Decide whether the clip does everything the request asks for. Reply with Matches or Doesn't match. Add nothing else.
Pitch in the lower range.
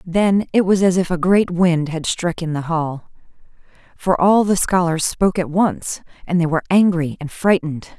Doesn't match